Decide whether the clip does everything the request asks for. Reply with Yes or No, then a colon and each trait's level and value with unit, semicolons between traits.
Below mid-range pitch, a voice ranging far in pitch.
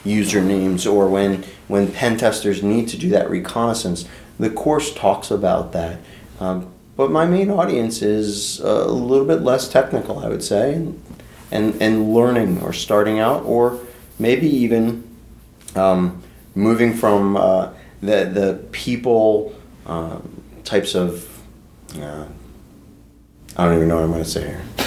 No: low, 105 Hz; average, 3.9 semitones